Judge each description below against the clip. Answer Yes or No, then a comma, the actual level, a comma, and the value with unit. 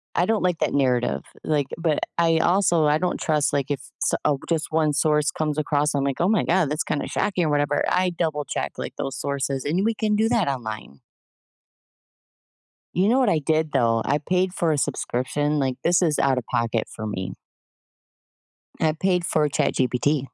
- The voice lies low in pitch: No, medium, 150 Hz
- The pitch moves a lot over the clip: No, average, 3.8 semitones